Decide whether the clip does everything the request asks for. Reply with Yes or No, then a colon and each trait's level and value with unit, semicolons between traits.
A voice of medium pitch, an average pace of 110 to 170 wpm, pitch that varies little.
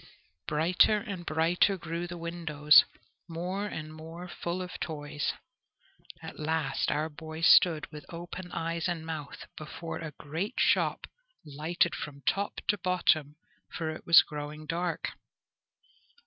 Yes: medium, 165 Hz; slow, 135 wpm; narrow, 2.3 semitones